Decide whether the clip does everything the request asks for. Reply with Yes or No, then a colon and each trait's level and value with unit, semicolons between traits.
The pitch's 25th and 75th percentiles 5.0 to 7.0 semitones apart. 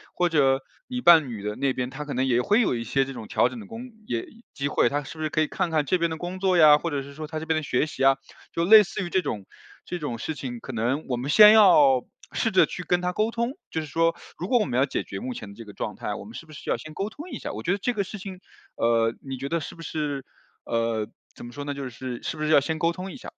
Yes: wide, 5.6 semitones